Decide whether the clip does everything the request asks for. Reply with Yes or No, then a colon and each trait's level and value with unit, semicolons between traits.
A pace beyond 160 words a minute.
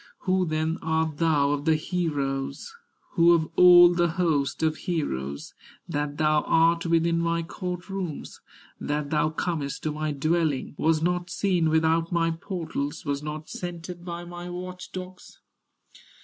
No: average, 150 wpm